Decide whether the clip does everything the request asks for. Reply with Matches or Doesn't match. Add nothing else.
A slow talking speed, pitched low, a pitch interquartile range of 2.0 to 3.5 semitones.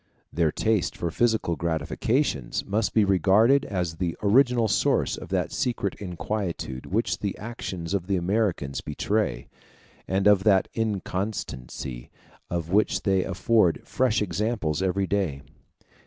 Doesn't match